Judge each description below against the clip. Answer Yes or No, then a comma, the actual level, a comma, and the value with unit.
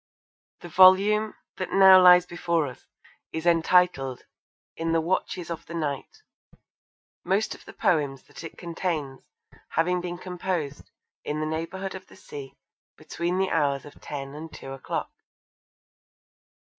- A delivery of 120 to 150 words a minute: Yes, average, 140 wpm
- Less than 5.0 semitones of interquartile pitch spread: Yes, average, 3.5 semitones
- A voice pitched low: No, medium, 170 Hz